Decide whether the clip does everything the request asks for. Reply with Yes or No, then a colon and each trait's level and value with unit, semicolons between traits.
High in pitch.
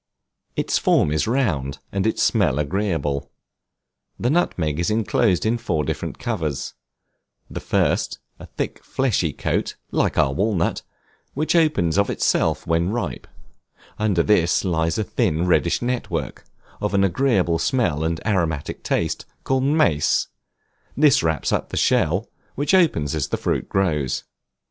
No: very low, 90 Hz